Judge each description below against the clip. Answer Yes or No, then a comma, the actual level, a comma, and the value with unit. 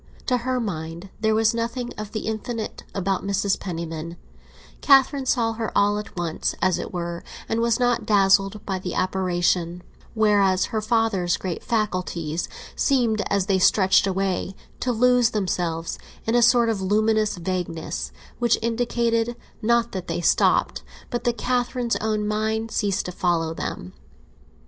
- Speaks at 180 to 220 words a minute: No, average, 150 wpm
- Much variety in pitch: No, average, 4.0 semitones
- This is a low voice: No, high, 210 Hz